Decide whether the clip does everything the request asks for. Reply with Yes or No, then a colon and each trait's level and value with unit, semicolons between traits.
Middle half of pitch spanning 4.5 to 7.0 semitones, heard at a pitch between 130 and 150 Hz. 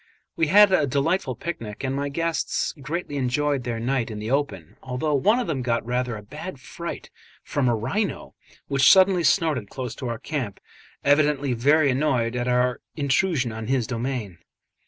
No: average, 3.7 semitones; low, 135 Hz